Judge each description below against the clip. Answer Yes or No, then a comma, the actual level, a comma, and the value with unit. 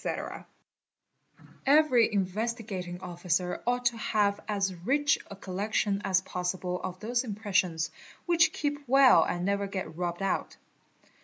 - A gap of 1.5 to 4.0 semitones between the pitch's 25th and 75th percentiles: No, average, 4.7 semitones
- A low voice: No, high, 200 Hz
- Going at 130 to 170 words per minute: Yes, slow, 135 wpm